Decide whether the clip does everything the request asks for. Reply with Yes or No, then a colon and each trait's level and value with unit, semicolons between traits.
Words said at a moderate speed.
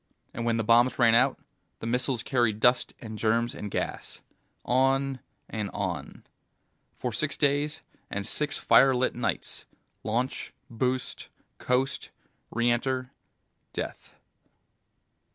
No: slow, 115 wpm